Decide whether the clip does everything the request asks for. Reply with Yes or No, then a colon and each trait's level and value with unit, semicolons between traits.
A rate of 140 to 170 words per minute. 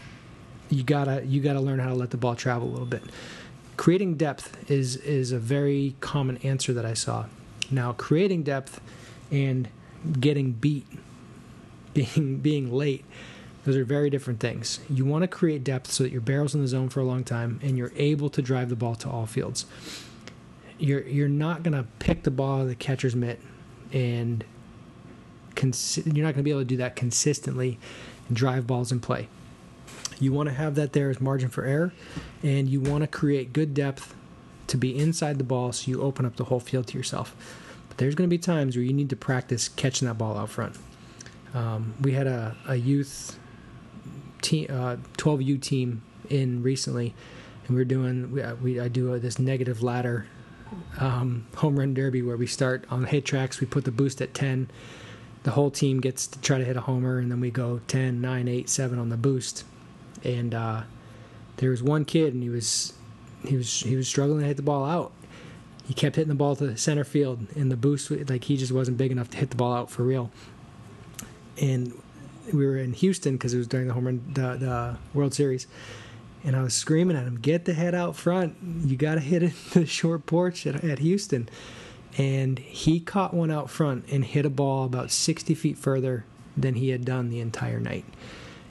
No: fast, 205 wpm